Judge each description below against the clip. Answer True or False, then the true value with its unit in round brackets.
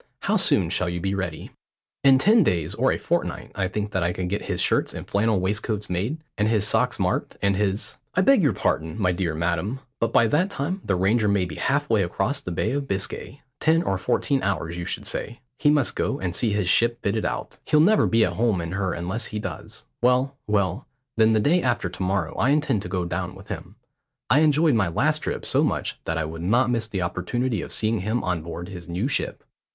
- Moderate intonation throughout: False (5.7 semitones)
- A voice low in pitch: True (105 Hz)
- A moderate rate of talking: False (230 wpm)